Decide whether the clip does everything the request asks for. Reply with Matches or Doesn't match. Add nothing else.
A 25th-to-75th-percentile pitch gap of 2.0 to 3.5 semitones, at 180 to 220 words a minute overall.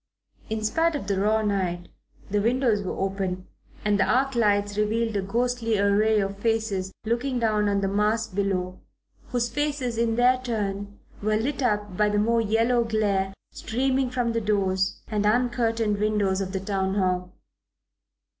Doesn't match